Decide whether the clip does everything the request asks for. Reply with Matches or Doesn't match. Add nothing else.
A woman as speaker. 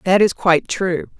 Matches